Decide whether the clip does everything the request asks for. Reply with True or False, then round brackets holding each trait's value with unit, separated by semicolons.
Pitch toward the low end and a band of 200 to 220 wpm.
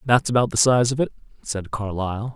True (115 Hz; 205 wpm)